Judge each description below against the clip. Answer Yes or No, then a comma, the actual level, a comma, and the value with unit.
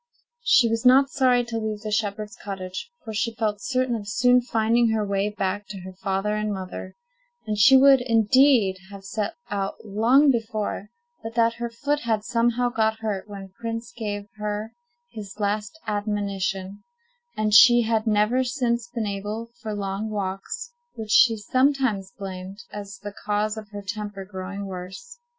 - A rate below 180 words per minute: Yes, average, 165 wpm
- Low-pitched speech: No, high, 215 Hz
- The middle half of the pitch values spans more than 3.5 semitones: No, average, 2.7 semitones